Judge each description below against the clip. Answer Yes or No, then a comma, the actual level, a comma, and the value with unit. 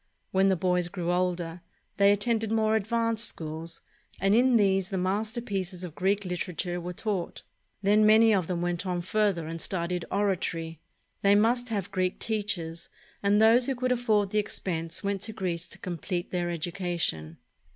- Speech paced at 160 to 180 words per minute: Yes, average, 165 wpm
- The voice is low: No, high, 190 Hz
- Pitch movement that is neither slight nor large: Yes, average, 3.4 semitones